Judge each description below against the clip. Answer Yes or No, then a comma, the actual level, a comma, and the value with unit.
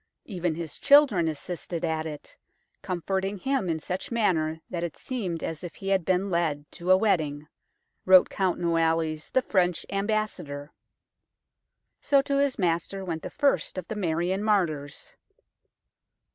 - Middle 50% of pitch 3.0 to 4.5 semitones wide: Yes, average, 3.5 semitones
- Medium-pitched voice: Yes, medium, 180 Hz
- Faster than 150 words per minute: No, average, 145 wpm